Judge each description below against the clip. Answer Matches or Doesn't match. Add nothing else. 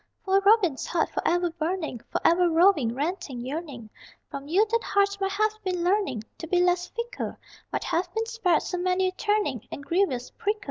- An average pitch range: Matches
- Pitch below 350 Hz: Doesn't match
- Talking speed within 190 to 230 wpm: Doesn't match